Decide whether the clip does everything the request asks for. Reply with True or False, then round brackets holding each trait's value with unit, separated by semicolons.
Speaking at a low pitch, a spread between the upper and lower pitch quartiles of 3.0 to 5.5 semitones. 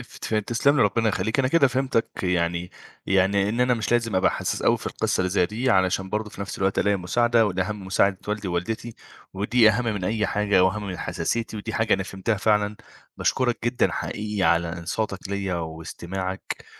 True (105 Hz; 3.3 semitones)